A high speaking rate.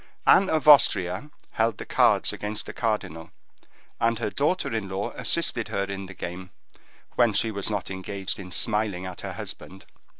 No: average, 170 wpm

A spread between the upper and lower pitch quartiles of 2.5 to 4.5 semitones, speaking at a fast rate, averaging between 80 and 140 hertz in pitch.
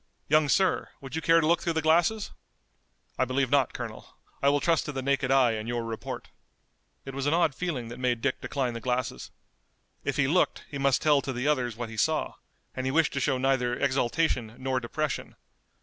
Yes: average, 3.6 semitones; fast, 210 wpm; low, 135 Hz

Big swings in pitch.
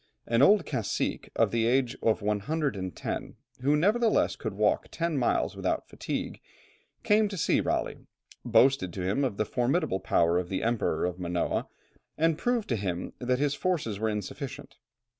Yes: wide, 6.8 semitones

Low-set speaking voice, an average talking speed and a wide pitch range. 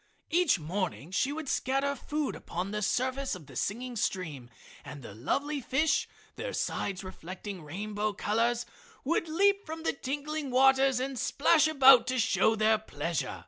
No: very high, 250 Hz; average, 155 wpm; wide, 6.4 semitones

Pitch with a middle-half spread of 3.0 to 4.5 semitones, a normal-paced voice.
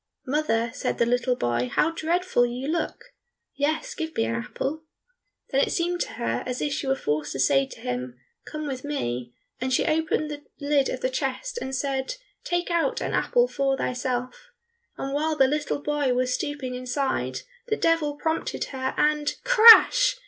Yes: average, 4.1 semitones; average, 180 wpm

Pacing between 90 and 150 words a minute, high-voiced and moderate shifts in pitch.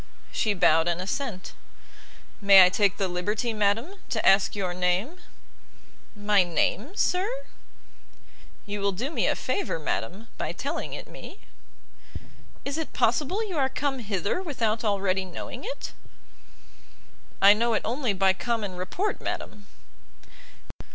No: slow, 135 wpm; high, 205 Hz; wide, 5.9 semitones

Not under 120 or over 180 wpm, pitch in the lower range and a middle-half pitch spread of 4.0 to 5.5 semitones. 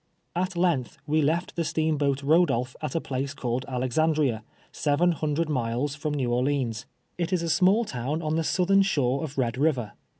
No: average, 175 wpm; medium, 150 Hz; average, 4.3 semitones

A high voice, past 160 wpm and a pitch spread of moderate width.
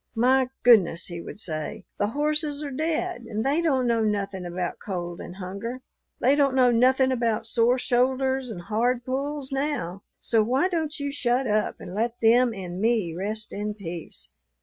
Yes: high, 235 Hz; average, 175 wpm; average, 4.6 semitones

